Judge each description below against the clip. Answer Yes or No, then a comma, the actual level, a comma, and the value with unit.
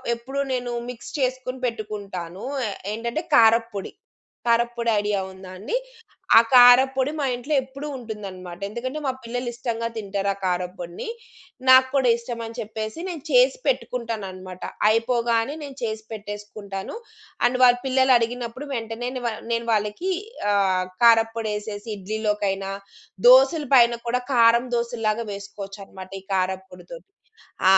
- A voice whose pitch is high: Yes, high, 230 Hz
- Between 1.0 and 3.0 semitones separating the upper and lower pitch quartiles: No, average, 3.5 semitones